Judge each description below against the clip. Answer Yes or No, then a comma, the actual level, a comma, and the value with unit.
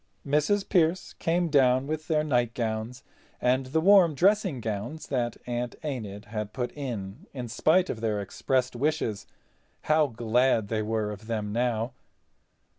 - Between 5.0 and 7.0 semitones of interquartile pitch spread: Yes, wide, 5.6 semitones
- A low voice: Yes, low, 125 Hz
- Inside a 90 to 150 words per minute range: Yes, average, 145 wpm